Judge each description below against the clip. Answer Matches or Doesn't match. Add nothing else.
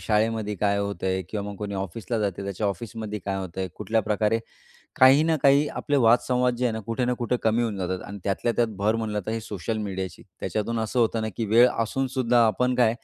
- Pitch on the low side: Matches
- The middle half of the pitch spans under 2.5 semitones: Doesn't match